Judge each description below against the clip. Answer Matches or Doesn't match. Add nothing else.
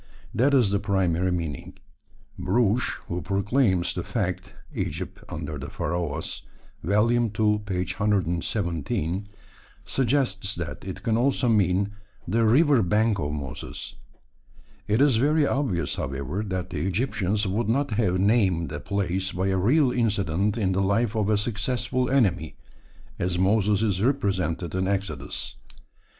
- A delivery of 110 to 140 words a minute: Matches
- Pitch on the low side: Matches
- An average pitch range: Matches